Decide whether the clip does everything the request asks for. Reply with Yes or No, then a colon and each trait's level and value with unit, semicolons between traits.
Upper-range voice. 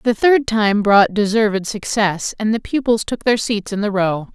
Yes: high, 215 Hz